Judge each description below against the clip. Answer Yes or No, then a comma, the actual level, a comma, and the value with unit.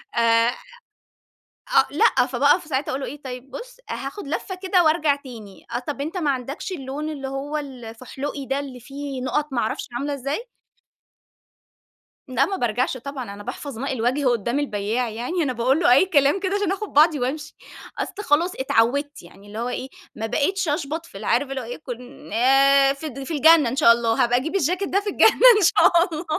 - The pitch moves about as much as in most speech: Yes, average, 3.8 semitones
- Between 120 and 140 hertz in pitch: No, very high, 275 Hz